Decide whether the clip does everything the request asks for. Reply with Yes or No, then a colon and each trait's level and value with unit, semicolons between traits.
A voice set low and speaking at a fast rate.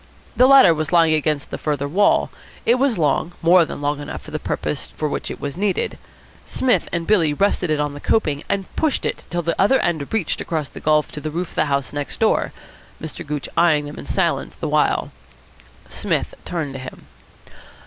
No: medium, 155 Hz; fast, 210 wpm